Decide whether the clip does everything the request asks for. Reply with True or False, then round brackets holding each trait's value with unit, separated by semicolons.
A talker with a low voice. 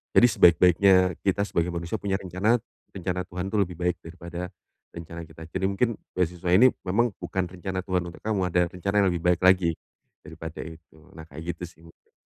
True (90 Hz)